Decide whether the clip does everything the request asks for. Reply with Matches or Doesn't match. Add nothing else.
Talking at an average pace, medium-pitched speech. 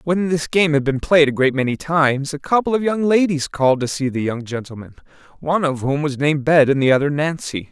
Doesn't match